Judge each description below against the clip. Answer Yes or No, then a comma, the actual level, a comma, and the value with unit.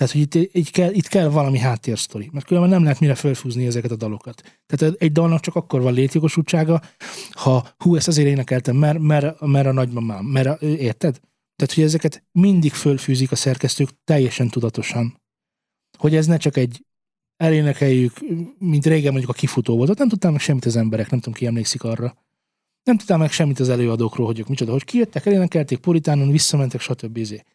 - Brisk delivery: Yes, fast, 185 wpm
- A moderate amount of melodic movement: Yes, average, 4.5 semitones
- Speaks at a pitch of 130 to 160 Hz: Yes, medium, 140 Hz